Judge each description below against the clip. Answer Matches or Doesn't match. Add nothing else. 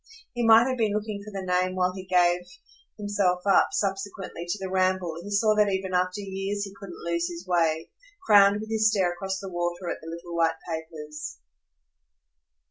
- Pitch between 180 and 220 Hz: Matches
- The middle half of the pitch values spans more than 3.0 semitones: Doesn't match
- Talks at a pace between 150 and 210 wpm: Matches